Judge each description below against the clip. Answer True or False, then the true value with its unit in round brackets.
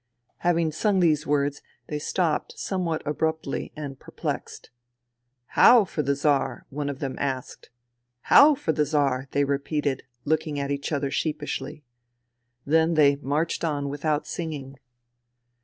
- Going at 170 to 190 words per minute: False (150 wpm)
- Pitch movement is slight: True (2.2 semitones)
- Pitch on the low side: False (145 Hz)